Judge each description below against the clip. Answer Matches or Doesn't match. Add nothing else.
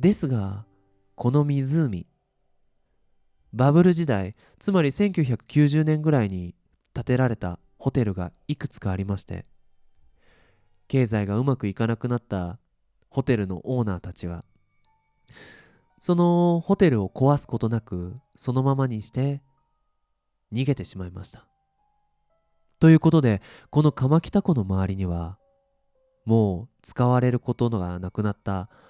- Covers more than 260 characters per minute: Doesn't match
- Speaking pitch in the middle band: Doesn't match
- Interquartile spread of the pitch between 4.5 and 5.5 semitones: Doesn't match